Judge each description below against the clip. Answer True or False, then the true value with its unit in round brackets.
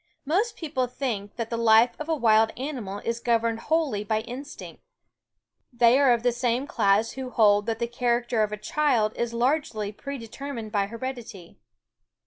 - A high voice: True (235 Hz)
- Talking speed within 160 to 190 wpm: True (165 wpm)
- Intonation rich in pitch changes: False (3.1 semitones)